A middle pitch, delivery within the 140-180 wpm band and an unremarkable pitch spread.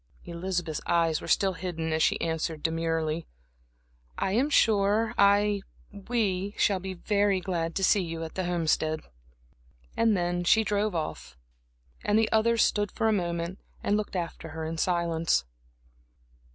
Yes: medium, 180 Hz; average, 150 wpm; average, 3.9 semitones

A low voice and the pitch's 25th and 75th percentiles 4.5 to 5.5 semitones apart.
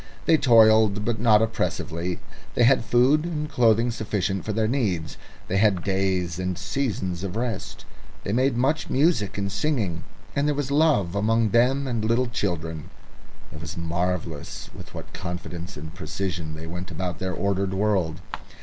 Yes: low, 100 Hz; average, 5.2 semitones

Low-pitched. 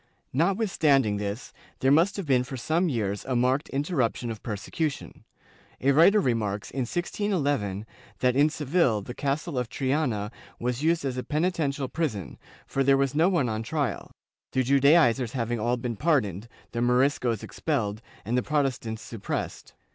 Yes: low, 130 Hz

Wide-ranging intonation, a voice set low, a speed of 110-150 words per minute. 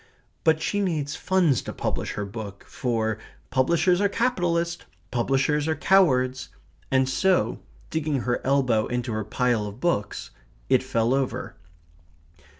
Yes: wide, 5.8 semitones; low, 130 Hz; slow, 135 wpm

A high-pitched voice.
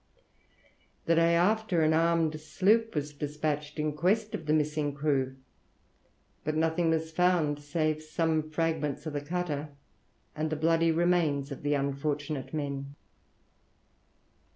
No: medium, 155 Hz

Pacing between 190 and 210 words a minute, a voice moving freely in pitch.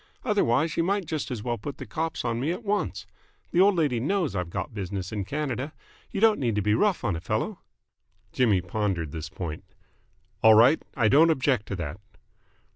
Yes: average, 200 wpm; wide, 7.9 semitones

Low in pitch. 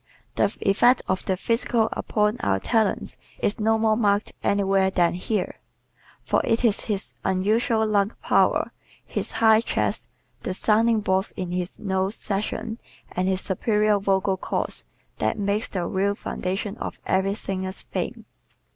No: high, 200 Hz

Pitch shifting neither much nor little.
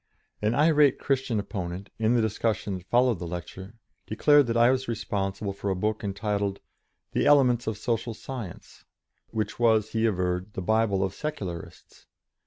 Yes: average, 3.5 semitones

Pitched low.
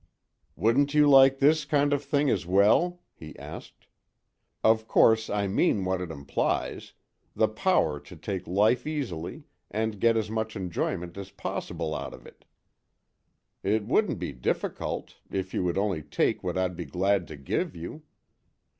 Yes: low, 100 Hz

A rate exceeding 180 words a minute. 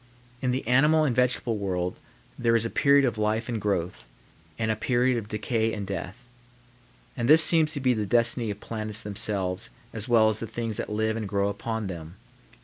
Yes: average, 200 wpm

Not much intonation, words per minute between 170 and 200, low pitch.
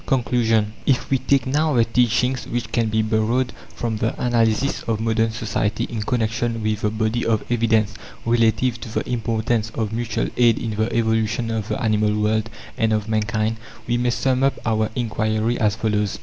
Yes: narrow, 1.7 semitones; average, 180 wpm; low, 115 Hz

